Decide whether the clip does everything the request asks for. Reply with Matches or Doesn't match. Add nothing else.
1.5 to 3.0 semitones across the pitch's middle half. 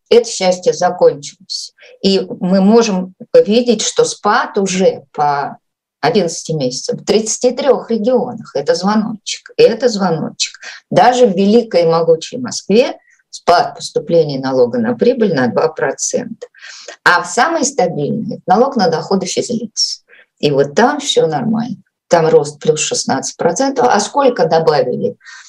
Doesn't match